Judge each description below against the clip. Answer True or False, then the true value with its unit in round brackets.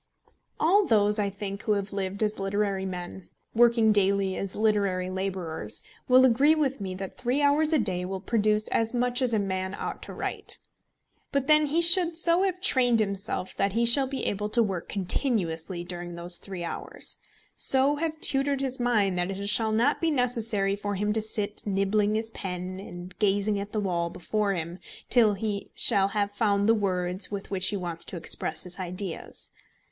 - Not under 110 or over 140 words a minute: False (190 wpm)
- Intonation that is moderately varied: True (4.0 semitones)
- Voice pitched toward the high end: True (205 Hz)